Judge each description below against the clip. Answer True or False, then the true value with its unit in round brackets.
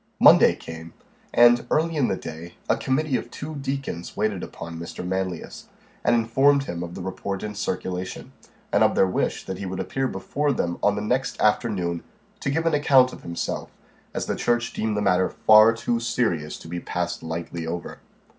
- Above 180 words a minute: True (190 wpm)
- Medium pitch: False (105 Hz)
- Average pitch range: False (6.4 semitones)